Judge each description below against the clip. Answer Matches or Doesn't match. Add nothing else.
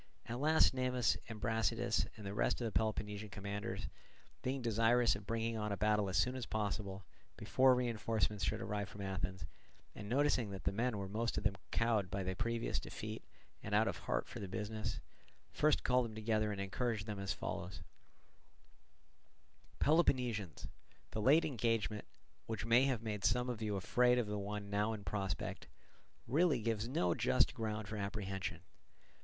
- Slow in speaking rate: Doesn't match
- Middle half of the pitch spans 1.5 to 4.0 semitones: Matches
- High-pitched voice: Doesn't match